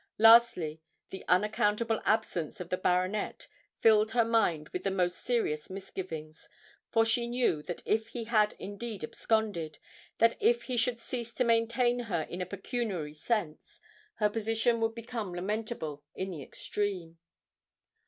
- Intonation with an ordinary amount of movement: Yes, average, 4.3 semitones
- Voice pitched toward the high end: Yes, high, 215 Hz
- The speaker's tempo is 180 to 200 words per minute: No, average, 145 wpm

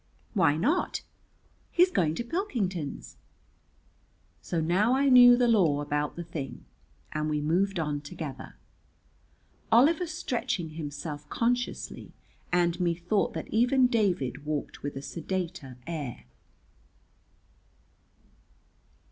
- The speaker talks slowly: Yes, slow, 105 wpm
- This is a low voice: No, medium, 175 Hz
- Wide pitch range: Yes, wide, 8.0 semitones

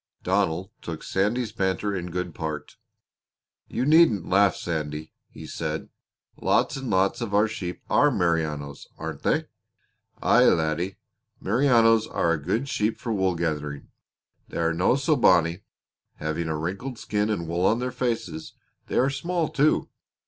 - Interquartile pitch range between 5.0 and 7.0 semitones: Yes, wide, 5.6 semitones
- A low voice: Yes, very low, 95 Hz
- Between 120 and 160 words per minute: Yes, average, 150 wpm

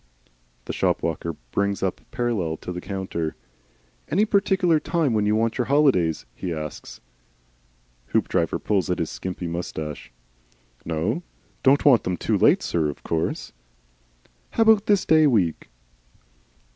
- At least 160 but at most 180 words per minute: No, average, 140 wpm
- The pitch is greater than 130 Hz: No, low, 100 Hz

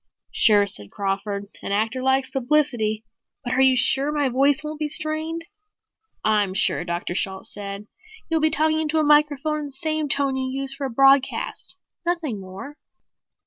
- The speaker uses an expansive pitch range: Yes, wide, 6.1 semitones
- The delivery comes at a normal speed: Yes, average, 170 wpm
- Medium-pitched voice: No, very high, 270 Hz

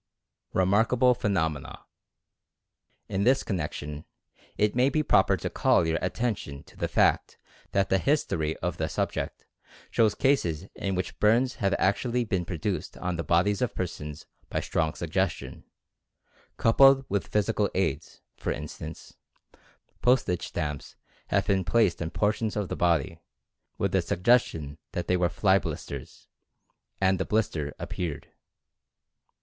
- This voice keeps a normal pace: Yes, average, 145 wpm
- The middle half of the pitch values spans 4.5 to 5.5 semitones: Yes, average, 5.0 semitones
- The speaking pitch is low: Yes, very low, 95 Hz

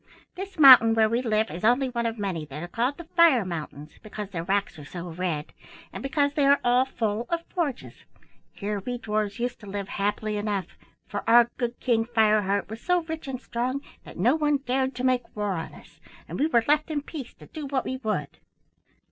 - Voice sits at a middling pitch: No, high, 235 Hz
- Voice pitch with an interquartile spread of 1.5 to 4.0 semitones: No, average, 4.8 semitones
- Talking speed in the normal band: No, fast, 215 wpm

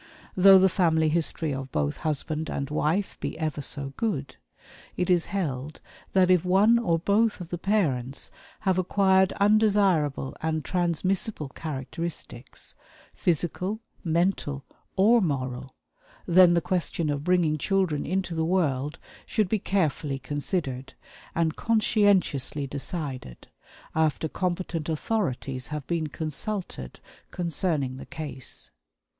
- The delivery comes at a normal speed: No, slow, 120 wpm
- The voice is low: No, medium, 165 Hz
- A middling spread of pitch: Yes, average, 4.7 semitones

